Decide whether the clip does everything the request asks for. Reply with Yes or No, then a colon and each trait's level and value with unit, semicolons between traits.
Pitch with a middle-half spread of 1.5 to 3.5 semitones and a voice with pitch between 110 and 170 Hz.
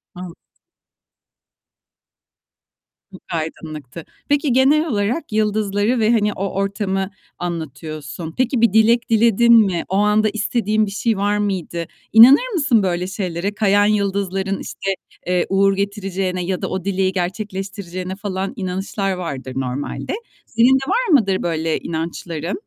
No: average, 3.2 semitones; high, 195 Hz